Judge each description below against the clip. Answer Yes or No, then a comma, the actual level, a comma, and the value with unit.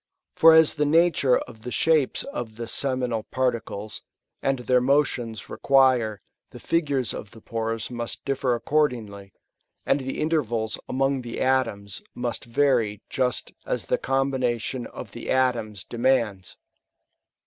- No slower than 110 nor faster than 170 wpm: Yes, average, 145 wpm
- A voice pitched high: No, low, 125 Hz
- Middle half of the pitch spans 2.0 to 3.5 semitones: Yes, average, 3.1 semitones